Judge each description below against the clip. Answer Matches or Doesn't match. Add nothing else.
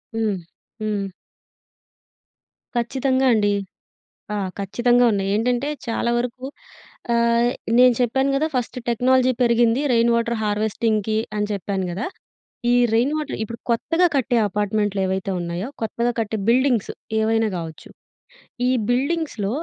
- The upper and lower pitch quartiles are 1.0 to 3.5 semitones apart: Matches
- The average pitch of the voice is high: Matches